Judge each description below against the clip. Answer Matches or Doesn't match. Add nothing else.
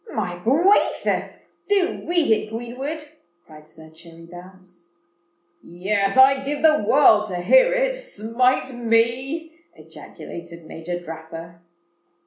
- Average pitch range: Doesn't match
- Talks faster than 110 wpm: Doesn't match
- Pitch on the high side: Matches